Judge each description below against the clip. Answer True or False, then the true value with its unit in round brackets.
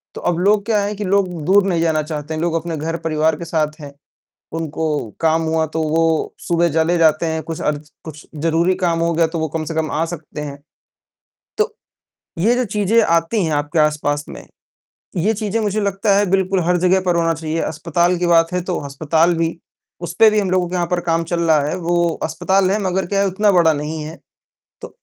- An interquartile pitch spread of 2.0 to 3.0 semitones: True (2.7 semitones)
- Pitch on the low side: False (165 Hz)